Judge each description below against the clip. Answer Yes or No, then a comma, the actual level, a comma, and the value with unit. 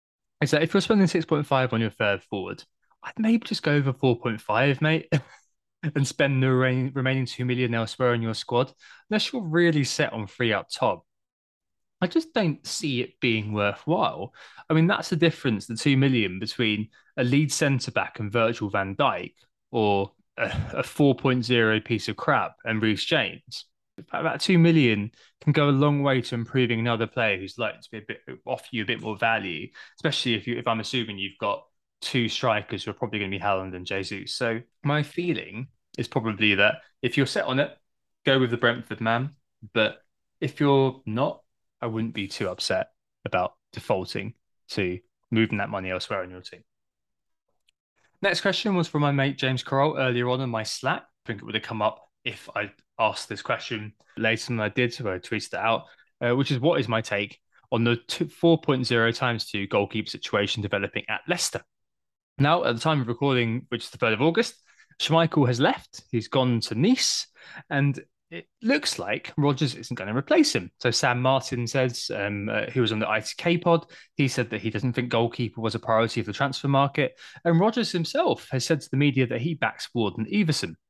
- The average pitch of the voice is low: Yes, low, 125 Hz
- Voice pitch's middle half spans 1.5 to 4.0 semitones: No, average, 4.6 semitones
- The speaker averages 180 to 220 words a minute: Yes, average, 195 wpm